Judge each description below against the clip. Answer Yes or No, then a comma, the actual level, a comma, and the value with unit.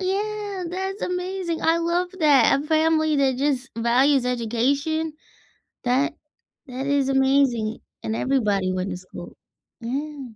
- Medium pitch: No, very high, 280 Hz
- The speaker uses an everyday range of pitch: Yes, average, 4.8 semitones